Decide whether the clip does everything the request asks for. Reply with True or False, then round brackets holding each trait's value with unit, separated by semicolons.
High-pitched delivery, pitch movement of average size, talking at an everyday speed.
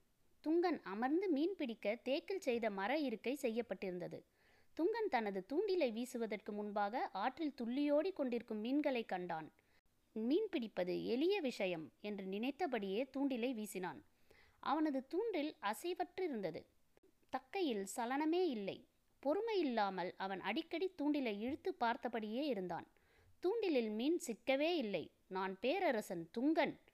False (255 Hz; 6.9 semitones; 105 wpm)